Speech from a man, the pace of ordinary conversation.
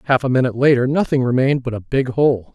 No: male; fast, 235 wpm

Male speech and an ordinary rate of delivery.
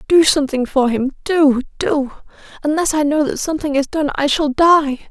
No: female; average, 175 wpm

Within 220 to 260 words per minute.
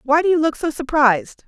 Yes: fast, 245 wpm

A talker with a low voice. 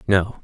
Yes: low, 100 Hz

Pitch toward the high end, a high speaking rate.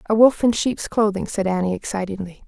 No: high, 205 Hz; average, 195 wpm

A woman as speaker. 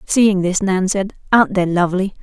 Yes: female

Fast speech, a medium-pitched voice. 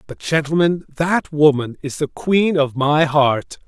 No: average, 165 wpm; medium, 150 Hz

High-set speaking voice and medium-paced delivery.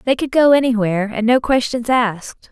Yes: high, 240 Hz; average, 190 wpm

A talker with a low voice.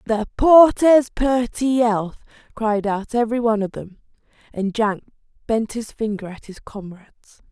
No: high, 225 Hz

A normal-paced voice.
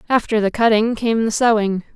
Yes: average, 185 wpm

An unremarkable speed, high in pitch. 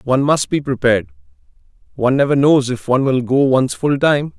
No: average, 190 wpm; low, 135 Hz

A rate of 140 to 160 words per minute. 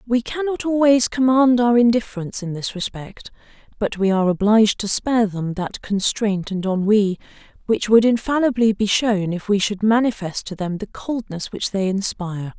No: average, 170 wpm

